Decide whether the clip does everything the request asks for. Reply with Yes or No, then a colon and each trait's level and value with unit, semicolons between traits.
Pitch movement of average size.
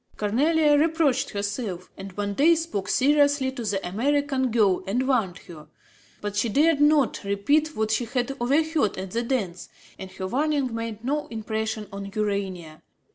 No: wide, 6.1 semitones